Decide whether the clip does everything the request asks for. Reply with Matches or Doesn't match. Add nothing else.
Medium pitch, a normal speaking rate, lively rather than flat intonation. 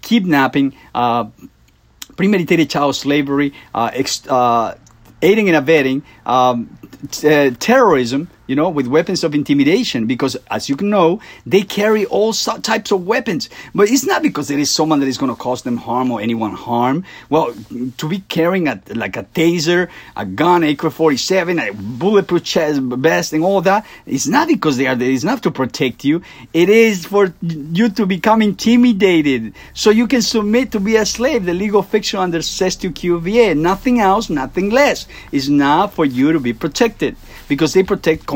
Matches